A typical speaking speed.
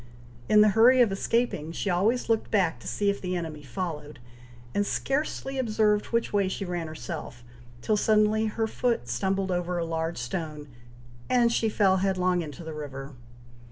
Yes: average, 170 wpm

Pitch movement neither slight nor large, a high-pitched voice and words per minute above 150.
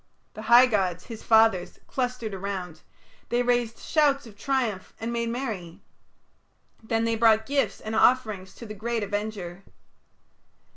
No: average, 3.2 semitones; high, 220 Hz; average, 140 wpm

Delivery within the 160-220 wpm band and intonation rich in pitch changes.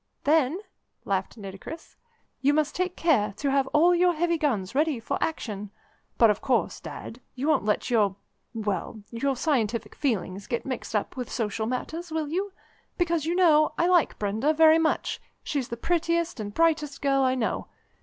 Yes: average, 175 wpm; wide, 6.4 semitones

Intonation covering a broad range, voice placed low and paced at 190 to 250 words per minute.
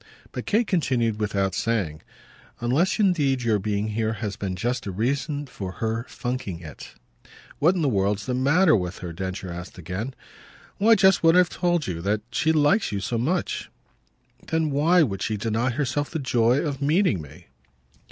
No: wide, 7.1 semitones; low, 120 Hz; average, 175 wpm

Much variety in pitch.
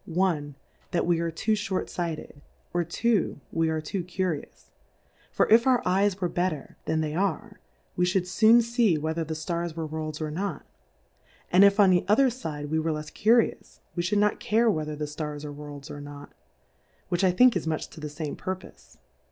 No: average, 4.4 semitones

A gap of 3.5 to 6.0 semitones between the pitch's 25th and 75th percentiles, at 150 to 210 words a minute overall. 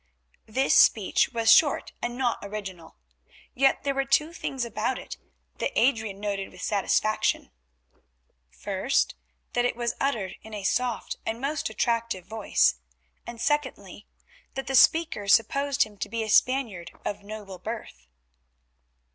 No: average, 4.7 semitones; average, 140 wpm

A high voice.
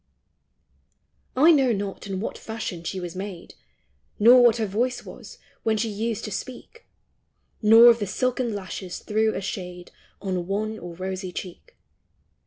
Yes: high, 210 Hz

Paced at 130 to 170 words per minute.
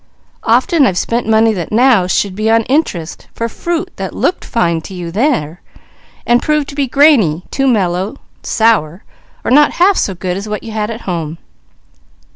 No: average, 180 wpm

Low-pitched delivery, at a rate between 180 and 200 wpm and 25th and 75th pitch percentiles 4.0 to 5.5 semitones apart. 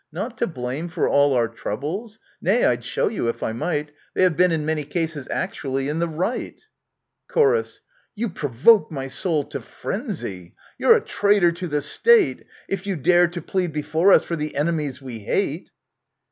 No: medium, 160 Hz; average, 190 wpm; average, 5.0 semitones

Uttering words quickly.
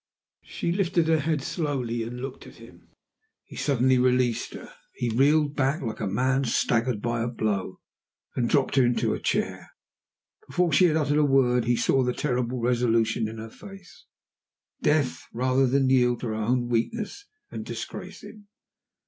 No: average, 165 wpm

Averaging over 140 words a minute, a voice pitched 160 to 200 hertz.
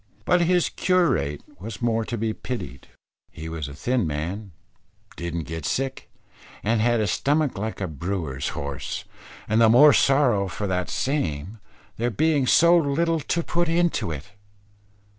No: average, 155 wpm; low, 110 Hz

